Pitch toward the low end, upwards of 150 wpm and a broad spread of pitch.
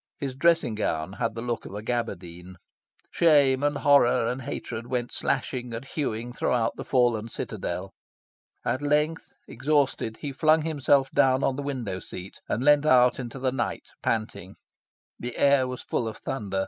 No: low, 125 Hz; average, 165 wpm; average, 3.8 semitones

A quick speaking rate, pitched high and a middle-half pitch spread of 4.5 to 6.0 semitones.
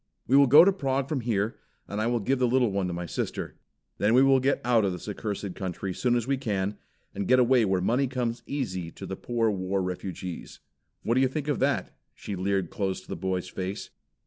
No: fast, 230 wpm; low, 110 Hz; average, 5.3 semitones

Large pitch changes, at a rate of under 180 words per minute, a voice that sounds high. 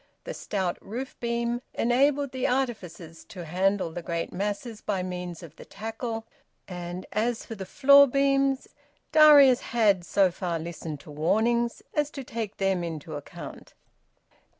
Yes: wide, 5.9 semitones; average, 150 wpm; high, 210 Hz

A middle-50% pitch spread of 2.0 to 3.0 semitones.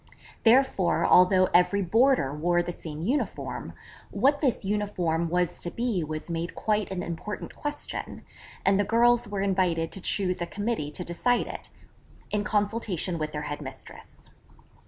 No: average, 3.9 semitones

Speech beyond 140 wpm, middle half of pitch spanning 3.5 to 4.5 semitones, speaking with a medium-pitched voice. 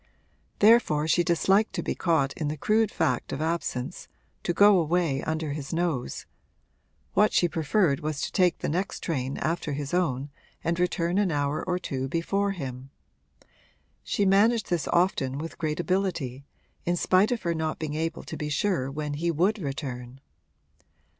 Yes: average, 165 wpm; average, 4.1 semitones; medium, 165 Hz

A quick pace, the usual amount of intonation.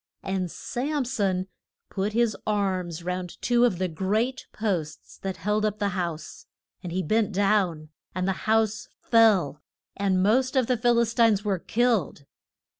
No: average, 160 wpm; average, 3.7 semitones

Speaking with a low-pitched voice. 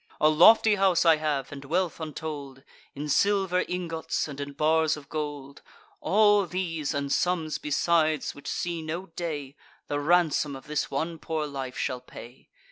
No: medium, 155 Hz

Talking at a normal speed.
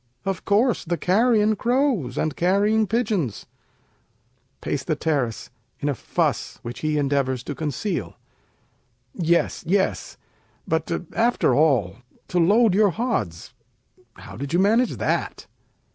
No: slow, 115 wpm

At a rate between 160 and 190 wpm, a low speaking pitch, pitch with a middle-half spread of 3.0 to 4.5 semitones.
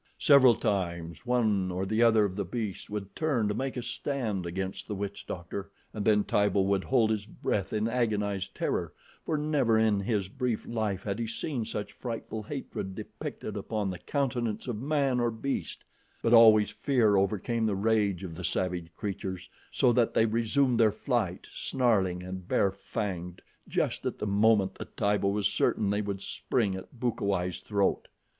Yes: average, 175 wpm; low, 105 Hz; average, 3.3 semitones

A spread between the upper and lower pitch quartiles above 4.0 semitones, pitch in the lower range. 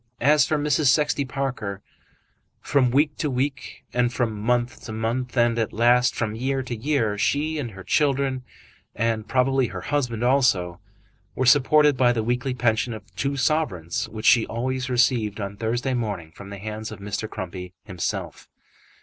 No: average, 3.7 semitones; low, 120 Hz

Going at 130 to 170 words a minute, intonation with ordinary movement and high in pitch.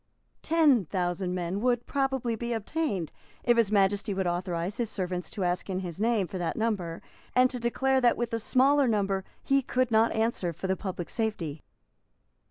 No: average, 180 wpm; average, 4.8 semitones; high, 210 Hz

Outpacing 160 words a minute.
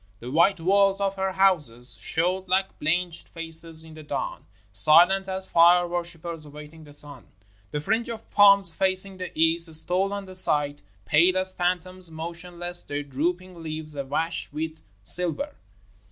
No: average, 155 wpm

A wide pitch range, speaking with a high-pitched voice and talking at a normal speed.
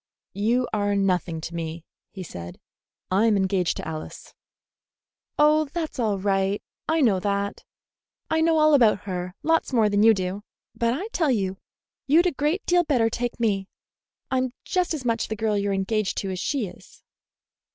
Yes: wide, 6.3 semitones; high, 215 Hz; average, 175 wpm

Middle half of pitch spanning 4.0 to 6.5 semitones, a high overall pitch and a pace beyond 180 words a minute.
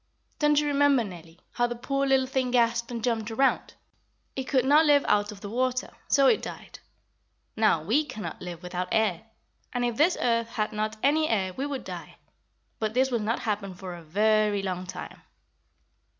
Yes: average, 4.5 semitones; high, 230 Hz; average, 190 wpm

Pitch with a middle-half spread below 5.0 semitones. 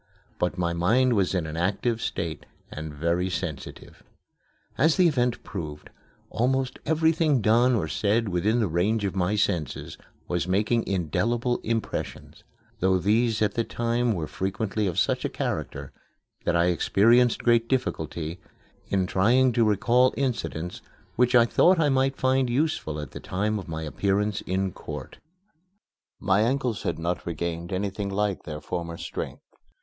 No: wide, 5.5 semitones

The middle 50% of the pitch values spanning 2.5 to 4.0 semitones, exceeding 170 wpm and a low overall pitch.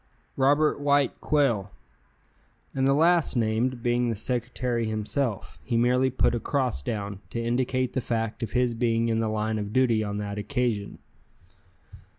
No: average, 2.9 semitones; average, 160 wpm; low, 120 Hz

